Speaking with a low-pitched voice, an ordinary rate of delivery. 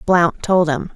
No: medium, 170 Hz; average, 190 wpm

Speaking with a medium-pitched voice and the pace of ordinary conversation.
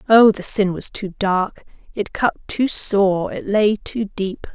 No: high, 200 Hz; average, 185 wpm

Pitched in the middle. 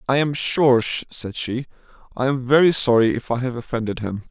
No: low, 125 Hz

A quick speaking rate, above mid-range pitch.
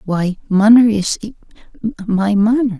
No: slow, 85 wpm; high, 210 Hz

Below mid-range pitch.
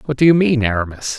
Yes: low, 130 Hz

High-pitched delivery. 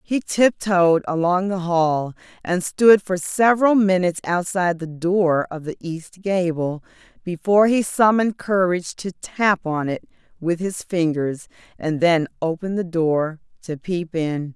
No: medium, 175 Hz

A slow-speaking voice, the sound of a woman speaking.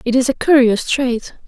No: fast, 205 wpm; female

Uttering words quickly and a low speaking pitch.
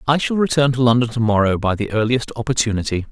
Yes: fast, 210 wpm; low, 120 Hz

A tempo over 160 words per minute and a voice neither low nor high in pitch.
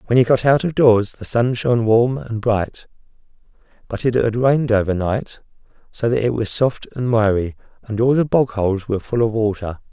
No: average, 200 wpm; low, 115 Hz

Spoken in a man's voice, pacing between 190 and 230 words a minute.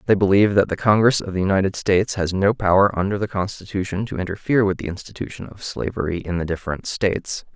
Yes: male; fast, 205 wpm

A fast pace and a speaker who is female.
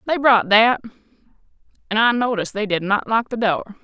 No: average, 190 wpm; female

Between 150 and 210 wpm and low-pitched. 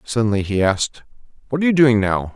Yes: fast, 205 wpm; low, 115 Hz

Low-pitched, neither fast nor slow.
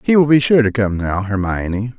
No: low, 115 Hz; fast, 240 wpm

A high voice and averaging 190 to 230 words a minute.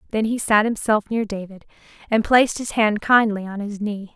Yes: high, 215 Hz; average, 200 wpm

